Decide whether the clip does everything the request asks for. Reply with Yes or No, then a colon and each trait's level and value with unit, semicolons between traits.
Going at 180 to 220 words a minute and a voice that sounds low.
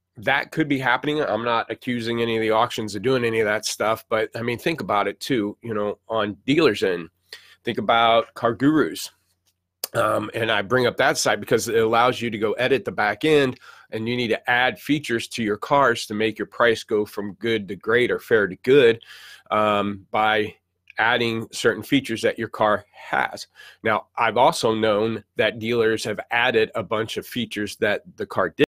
Yes: average, 200 wpm; low, 115 Hz